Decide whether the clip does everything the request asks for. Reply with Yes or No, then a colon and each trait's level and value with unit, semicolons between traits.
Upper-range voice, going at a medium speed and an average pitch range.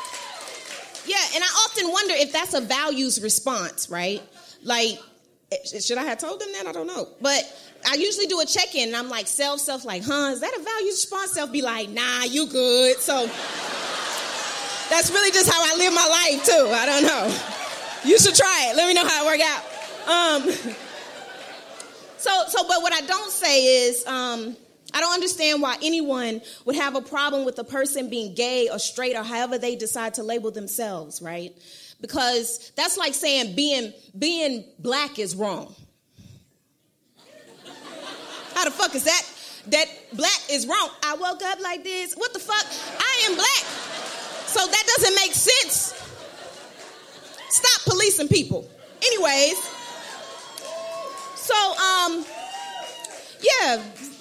No: very high, 295 Hz; average, 160 wpm; wide, 6.7 semitones